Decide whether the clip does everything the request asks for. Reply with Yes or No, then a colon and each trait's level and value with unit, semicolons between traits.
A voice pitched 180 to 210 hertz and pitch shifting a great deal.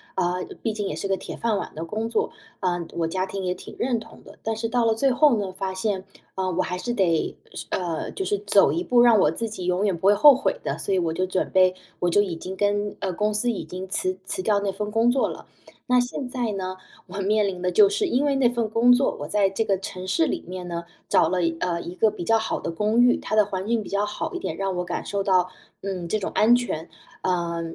No: high, 195 Hz; average, 3.7 semitones